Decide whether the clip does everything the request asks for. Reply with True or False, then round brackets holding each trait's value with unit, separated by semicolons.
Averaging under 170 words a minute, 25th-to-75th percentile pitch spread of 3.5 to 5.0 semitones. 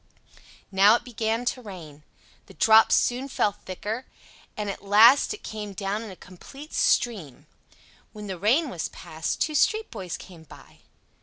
True (160 wpm; 4.2 semitones)